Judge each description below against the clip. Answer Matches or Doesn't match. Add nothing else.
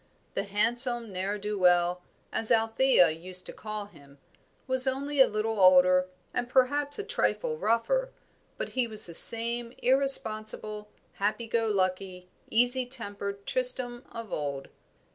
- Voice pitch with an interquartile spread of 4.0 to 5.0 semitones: Matches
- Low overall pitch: Doesn't match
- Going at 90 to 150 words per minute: Matches